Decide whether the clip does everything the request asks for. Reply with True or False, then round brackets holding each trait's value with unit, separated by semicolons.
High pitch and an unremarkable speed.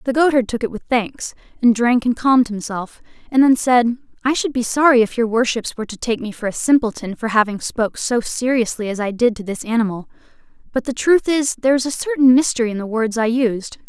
False (240 Hz; 230 wpm)